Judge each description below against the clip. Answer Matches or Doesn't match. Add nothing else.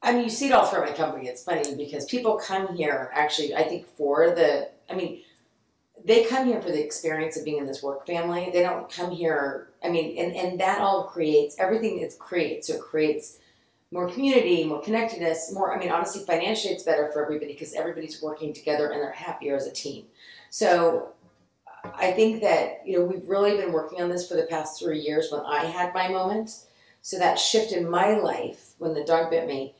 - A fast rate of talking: Matches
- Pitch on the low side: Doesn't match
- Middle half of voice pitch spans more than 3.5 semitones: Matches